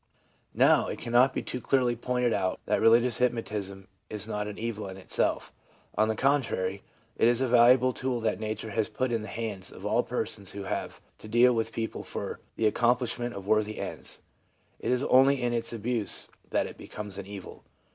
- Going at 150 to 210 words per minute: Yes, average, 195 wpm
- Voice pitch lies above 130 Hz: No, low, 115 Hz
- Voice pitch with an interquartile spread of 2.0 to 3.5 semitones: Yes, average, 2.7 semitones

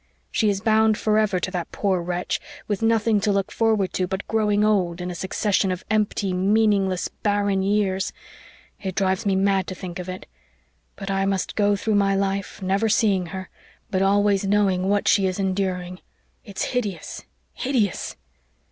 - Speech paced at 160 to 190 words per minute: Yes, average, 170 wpm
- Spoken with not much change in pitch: Yes, narrow, 1.8 semitones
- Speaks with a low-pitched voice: No, high, 195 Hz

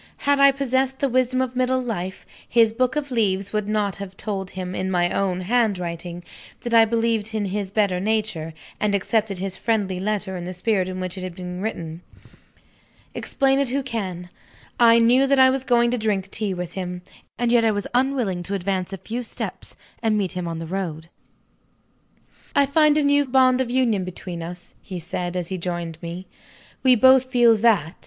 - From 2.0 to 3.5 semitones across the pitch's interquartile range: No, average, 5.0 semitones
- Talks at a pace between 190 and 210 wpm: Yes, average, 195 wpm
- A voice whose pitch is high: Yes, high, 210 Hz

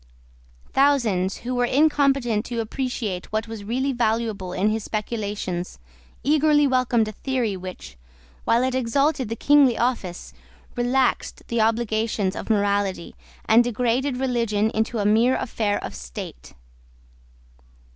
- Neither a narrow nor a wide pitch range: Yes, average, 3.5 semitones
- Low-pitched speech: No, high, 230 Hz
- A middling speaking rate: No, slow, 125 wpm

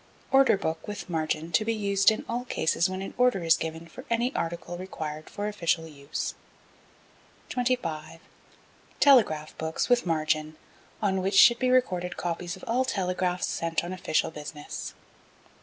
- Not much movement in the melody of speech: No, average, 5.1 semitones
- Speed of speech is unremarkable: Yes, average, 155 wpm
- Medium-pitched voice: Yes, medium, 180 Hz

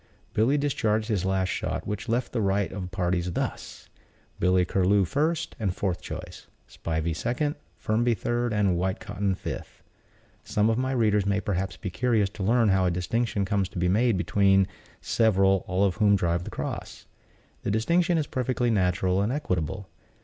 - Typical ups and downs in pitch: Yes, average, 3.8 semitones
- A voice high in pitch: No, low, 100 Hz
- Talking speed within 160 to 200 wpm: Yes, average, 170 wpm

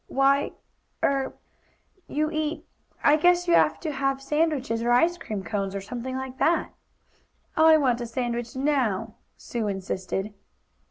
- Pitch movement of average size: Yes, average, 4.7 semitones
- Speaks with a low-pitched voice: No, very high, 265 Hz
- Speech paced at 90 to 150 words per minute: Yes, average, 145 wpm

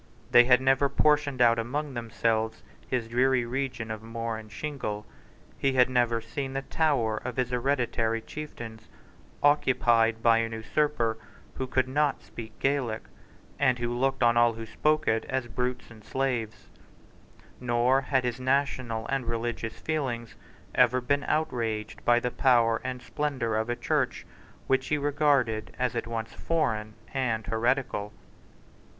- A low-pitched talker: Yes, low, 120 Hz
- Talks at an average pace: Yes, average, 150 wpm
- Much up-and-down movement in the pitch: No, average, 2.8 semitones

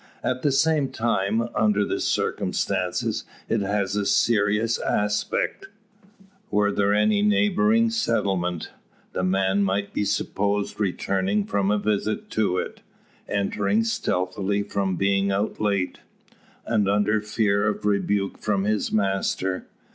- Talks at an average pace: No, slow, 125 wpm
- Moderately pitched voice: No, low, 105 Hz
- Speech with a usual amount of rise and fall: No, narrow, 1.7 semitones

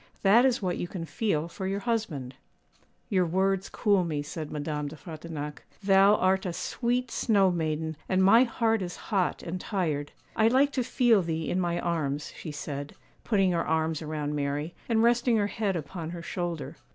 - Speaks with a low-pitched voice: No, medium, 180 Hz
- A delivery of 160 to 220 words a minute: Yes, average, 185 wpm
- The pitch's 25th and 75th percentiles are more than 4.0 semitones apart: Yes, average, 4.6 semitones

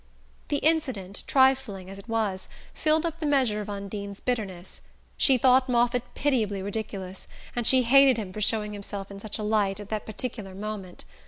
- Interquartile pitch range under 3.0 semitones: No, average, 4.4 semitones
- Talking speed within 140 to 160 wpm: No, average, 175 wpm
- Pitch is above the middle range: Yes, high, 215 Hz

